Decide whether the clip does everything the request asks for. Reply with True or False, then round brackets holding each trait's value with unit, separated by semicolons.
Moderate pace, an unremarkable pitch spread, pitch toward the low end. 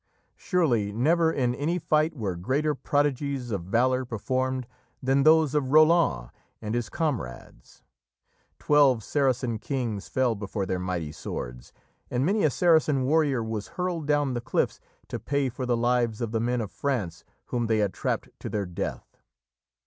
True (160 wpm; 4.9 semitones; 130 Hz)